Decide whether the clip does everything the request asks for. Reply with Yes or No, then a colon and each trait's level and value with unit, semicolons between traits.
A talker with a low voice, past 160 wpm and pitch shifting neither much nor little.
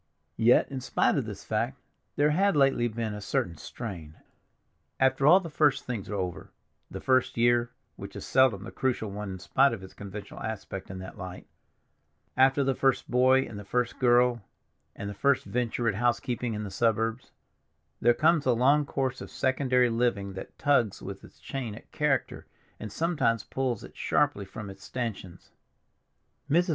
Yes: low, 120 Hz; average, 175 wpm; average, 4.3 semitones